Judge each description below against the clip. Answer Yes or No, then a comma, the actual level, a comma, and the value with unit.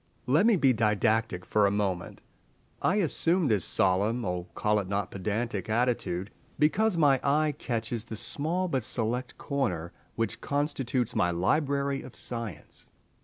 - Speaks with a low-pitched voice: Yes, low, 115 Hz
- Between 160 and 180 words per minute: No, slow, 135 wpm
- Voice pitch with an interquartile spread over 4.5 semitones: Yes, wide, 5.5 semitones